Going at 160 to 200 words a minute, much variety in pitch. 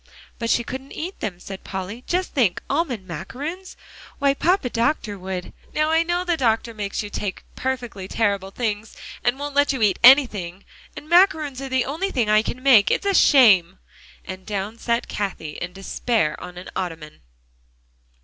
Yes: average, 175 wpm; wide, 6.5 semitones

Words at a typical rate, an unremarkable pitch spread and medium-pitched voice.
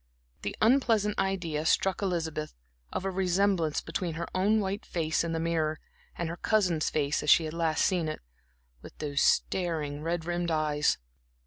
Yes: average, 165 wpm; average, 3.5 semitones; medium, 170 Hz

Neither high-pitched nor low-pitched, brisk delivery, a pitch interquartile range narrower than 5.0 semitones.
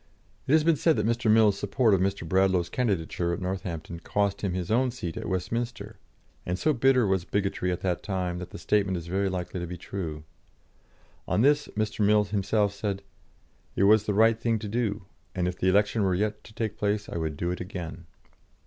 No: low, 100 Hz; fast, 210 wpm; average, 3.4 semitones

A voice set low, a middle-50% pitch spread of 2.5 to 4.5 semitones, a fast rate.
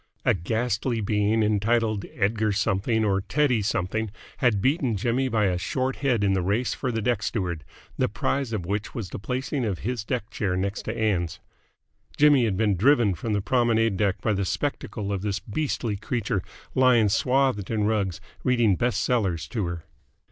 No: low, 110 Hz; average, 3.6 semitones; average, 180 wpm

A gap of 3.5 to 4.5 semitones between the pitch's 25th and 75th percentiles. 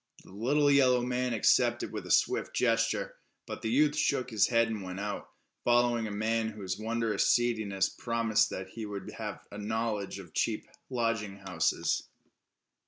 No: average, 2.8 semitones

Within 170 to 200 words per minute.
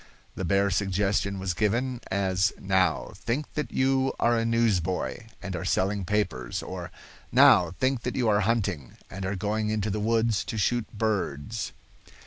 No: average, 160 wpm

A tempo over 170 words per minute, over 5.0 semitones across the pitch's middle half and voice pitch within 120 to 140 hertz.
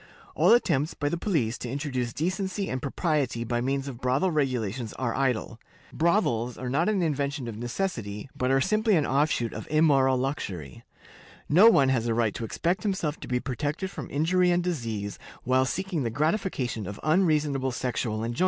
Yes: average, 180 wpm; wide, 5.5 semitones; low, 135 Hz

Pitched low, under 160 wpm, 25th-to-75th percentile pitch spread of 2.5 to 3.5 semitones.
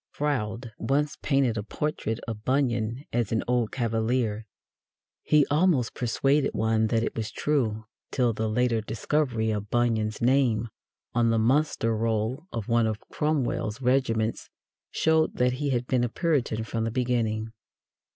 Yes: low, 120 Hz; average, 150 wpm; average, 3.2 semitones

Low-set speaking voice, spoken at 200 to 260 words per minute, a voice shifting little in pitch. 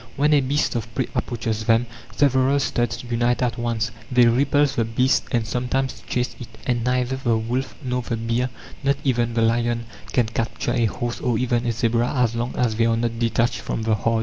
Yes: low, 120 Hz; fast, 205 wpm; narrow, 1.7 semitones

